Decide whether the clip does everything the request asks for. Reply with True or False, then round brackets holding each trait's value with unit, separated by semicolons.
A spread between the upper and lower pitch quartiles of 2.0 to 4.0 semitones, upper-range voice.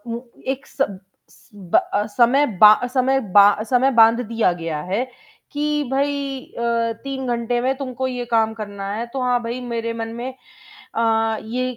True (2.7 semitones; 235 Hz)